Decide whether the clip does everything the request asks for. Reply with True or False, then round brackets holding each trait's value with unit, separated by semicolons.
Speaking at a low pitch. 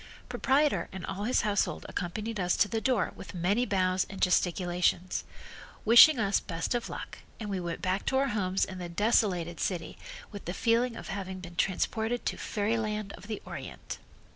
False (200 Hz)